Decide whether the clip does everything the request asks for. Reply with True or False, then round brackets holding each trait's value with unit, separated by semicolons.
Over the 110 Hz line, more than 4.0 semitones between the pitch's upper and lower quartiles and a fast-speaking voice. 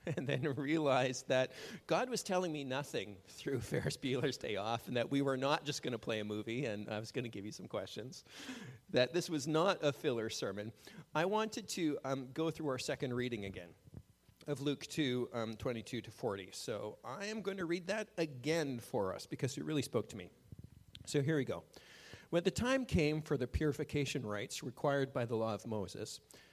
True (135 Hz; 5.1 semitones; 210 wpm)